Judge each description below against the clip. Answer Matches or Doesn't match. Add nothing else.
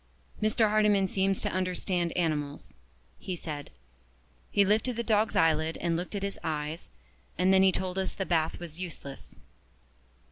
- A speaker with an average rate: Matches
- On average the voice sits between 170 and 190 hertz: Matches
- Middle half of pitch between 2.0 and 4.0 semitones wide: Matches